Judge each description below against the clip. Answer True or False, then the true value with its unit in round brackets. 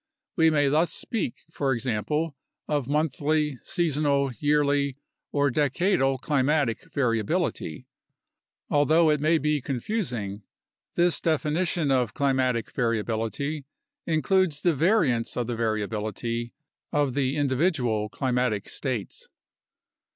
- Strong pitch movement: False (4.2 semitones)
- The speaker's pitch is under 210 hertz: True (140 Hz)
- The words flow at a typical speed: False (105 wpm)